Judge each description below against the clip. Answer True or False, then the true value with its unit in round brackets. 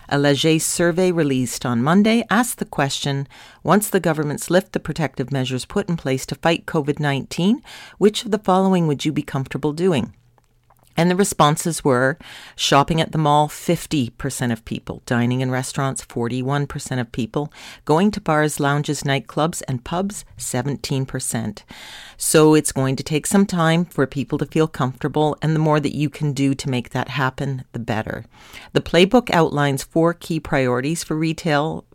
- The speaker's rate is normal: True (170 wpm)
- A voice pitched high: False (150 Hz)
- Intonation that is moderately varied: True (3.8 semitones)